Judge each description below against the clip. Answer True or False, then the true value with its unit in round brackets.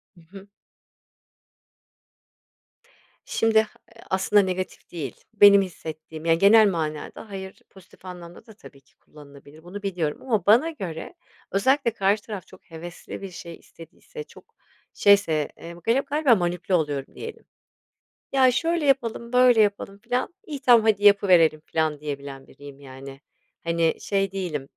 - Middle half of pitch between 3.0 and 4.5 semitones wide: False (5.4 semitones)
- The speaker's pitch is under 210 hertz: True (190 Hz)